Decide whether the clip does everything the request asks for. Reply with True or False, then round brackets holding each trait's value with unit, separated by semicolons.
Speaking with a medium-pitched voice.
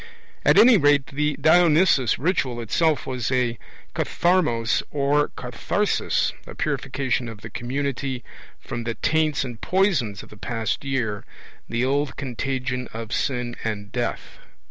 False (130 Hz)